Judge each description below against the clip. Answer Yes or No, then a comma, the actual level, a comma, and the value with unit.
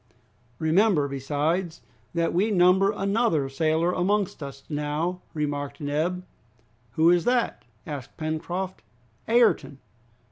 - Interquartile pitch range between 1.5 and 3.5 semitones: No, average, 4.2 semitones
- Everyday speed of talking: No, slow, 105 wpm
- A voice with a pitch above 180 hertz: No, medium, 165 Hz